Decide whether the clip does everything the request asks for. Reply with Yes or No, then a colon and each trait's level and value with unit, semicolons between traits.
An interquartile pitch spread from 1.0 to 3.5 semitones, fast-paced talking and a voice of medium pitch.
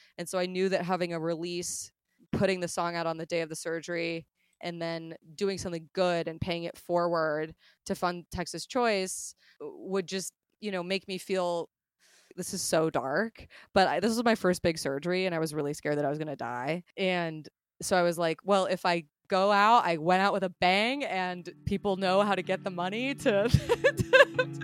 Yes: narrow, 2.6 semitones; fast, 210 wpm; medium, 180 Hz